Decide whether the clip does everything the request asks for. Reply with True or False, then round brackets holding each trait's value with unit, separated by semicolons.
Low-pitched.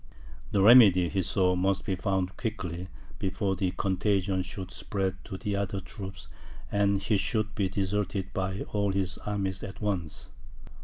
True (95 Hz)